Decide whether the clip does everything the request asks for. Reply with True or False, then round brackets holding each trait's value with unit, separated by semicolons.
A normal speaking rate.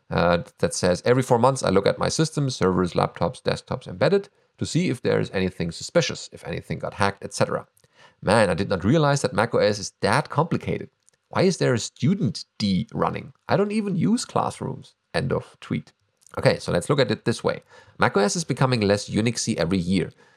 True (195 wpm)